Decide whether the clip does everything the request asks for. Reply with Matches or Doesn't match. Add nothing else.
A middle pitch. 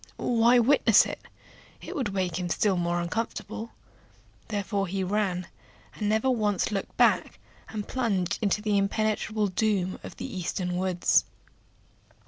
Doesn't match